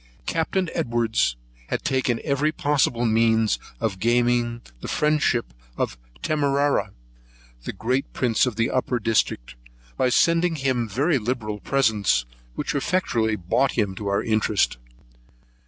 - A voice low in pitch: Yes, low, 120 Hz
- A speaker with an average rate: No, slow, 130 wpm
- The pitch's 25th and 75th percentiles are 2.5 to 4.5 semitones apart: Yes, average, 3.9 semitones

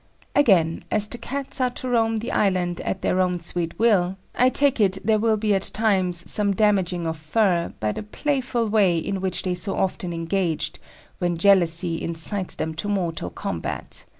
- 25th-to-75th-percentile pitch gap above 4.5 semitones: No, average, 4.0 semitones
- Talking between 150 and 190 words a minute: Yes, average, 180 wpm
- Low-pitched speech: No, high, 190 Hz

